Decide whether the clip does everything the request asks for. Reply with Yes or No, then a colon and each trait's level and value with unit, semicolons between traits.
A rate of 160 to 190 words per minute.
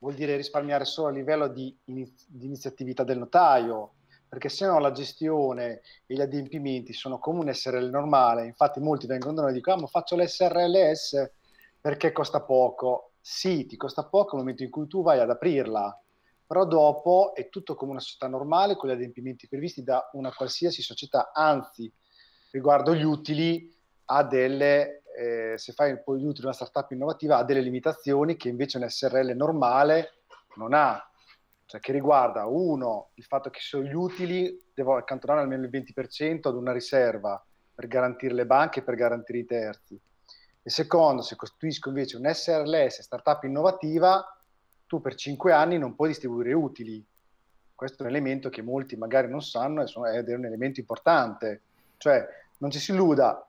Yes: fast, 170 wpm